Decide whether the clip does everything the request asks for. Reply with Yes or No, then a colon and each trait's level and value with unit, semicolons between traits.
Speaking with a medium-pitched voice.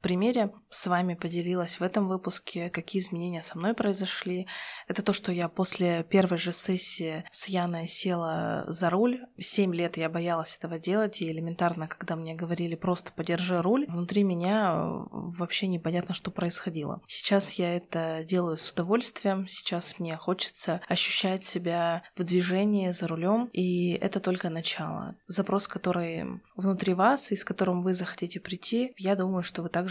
Yes: medium, 180 Hz